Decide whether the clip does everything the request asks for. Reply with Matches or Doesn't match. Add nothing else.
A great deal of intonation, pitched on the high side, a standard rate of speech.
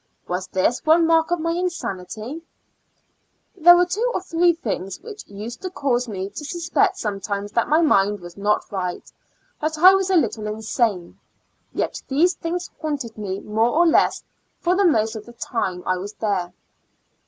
Matches